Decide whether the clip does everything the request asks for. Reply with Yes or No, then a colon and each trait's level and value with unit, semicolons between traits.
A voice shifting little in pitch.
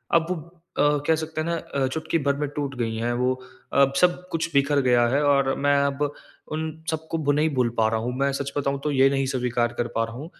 No: average, 3.5 semitones